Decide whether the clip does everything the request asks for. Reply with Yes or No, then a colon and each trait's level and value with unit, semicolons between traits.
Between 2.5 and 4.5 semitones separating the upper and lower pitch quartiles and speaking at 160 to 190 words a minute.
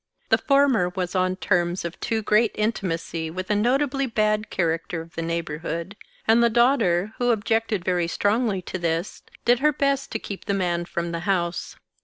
No: average, 4.9 semitones; average, 180 wpm